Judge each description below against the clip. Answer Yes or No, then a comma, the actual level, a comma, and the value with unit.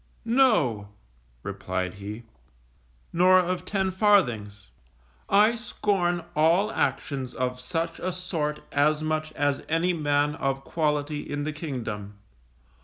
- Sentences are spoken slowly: Yes, slow, 115 wpm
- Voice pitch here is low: No, medium, 155 Hz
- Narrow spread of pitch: No, average, 5.3 semitones